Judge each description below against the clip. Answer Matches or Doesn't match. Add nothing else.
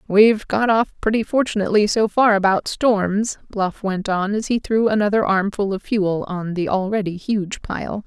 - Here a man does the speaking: Doesn't match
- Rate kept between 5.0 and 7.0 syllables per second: Doesn't match